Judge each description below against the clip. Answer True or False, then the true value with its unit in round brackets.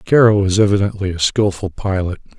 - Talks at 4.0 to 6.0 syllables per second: True (5.6 syllables/s)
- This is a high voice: False (100 Hz)